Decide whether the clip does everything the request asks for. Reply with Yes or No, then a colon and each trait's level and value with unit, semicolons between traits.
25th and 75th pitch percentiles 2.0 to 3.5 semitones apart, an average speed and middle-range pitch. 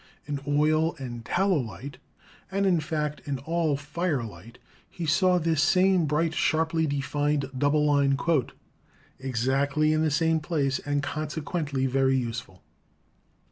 No: average, 2.9 semitones; slow, 130 wpm; medium, 150 Hz